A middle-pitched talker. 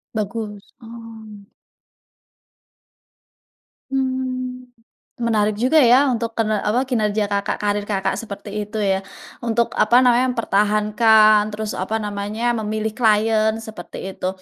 No: high, 215 Hz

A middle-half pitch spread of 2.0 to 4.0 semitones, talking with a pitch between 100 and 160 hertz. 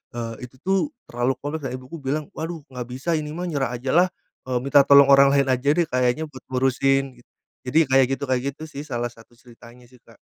Yes: average, 2.8 semitones; low, 135 Hz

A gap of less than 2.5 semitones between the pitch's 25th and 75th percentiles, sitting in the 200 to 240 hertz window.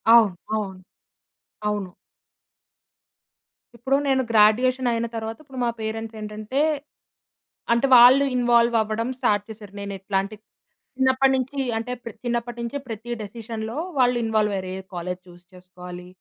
No: average, 2.9 semitones; high, 225 Hz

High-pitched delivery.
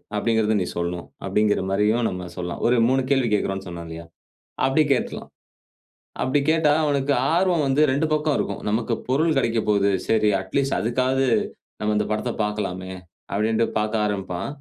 No: low, 110 Hz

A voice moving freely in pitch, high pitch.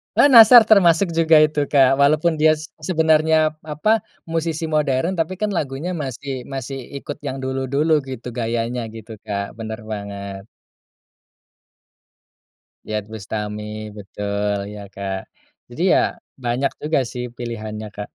No: wide, 6.5 semitones; low, 135 Hz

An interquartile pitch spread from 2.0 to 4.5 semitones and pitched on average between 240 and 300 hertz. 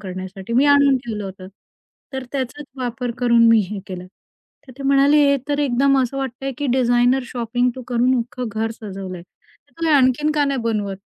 Yes: average, 3.4 semitones; very high, 250 Hz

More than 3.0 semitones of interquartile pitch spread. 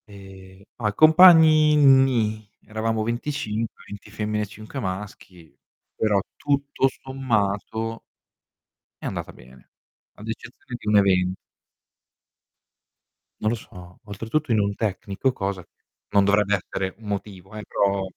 Yes: average, 3.5 semitones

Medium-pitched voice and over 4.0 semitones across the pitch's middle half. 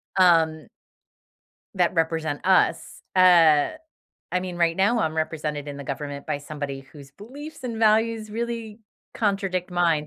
Yes: medium, 175 Hz; wide, 5.5 semitones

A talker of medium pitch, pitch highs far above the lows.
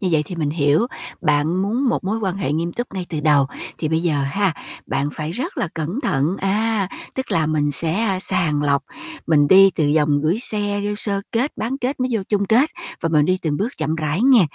Yes: medium, 180 Hz; wide, 5.7 semitones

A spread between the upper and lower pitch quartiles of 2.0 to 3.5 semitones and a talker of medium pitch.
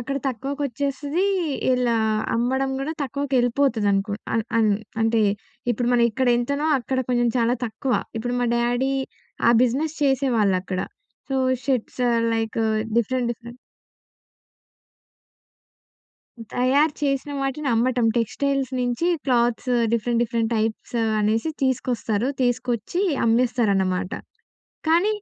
No: average, 2.9 semitones; high, 245 Hz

